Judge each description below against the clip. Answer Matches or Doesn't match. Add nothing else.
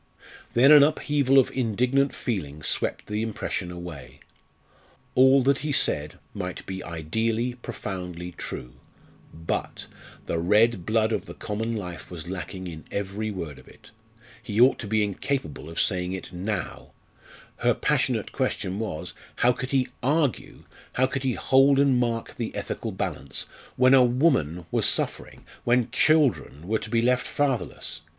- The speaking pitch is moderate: Doesn't match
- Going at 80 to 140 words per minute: Doesn't match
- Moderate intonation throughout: Doesn't match